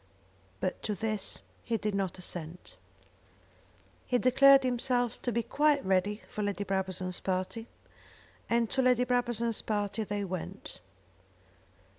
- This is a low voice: No, high, 215 Hz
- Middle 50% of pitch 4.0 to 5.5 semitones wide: Yes, average, 4.3 semitones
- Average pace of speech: No, slow, 125 wpm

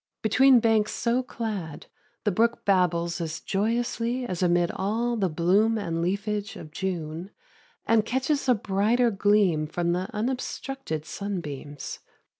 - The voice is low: No, high, 200 Hz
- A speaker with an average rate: No, slow, 130 wpm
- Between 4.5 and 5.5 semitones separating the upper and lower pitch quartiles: Yes, average, 5.1 semitones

